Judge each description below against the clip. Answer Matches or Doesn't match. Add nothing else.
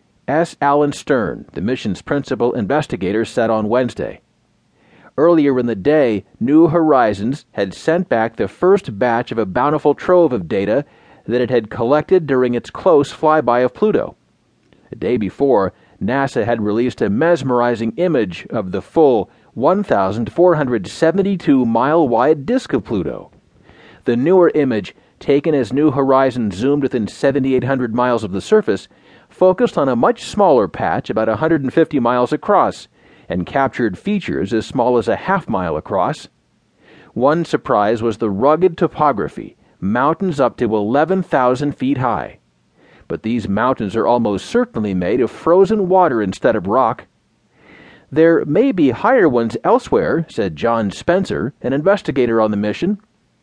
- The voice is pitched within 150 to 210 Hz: Doesn't match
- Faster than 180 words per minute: Doesn't match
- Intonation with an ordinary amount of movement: Doesn't match